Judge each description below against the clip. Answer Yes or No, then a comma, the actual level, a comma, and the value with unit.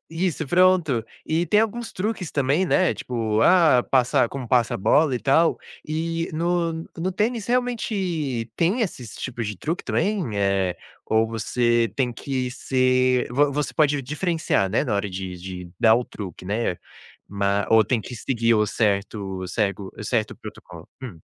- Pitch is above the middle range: No, low, 125 Hz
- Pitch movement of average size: No, wide, 7.4 semitones